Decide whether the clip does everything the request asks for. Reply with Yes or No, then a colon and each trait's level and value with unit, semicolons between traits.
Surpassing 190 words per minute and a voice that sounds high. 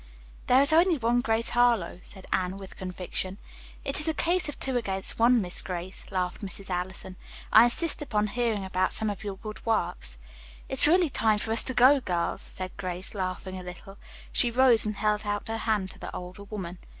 Yes: average, 200 wpm; high, 210 Hz